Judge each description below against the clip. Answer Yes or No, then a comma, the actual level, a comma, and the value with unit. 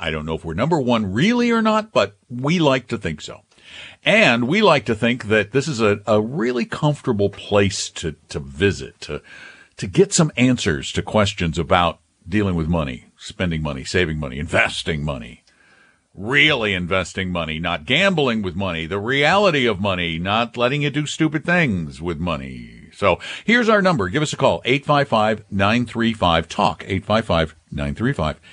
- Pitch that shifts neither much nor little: No, wide, 7.6 semitones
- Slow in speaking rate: No, average, 165 wpm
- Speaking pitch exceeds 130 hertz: No, low, 105 Hz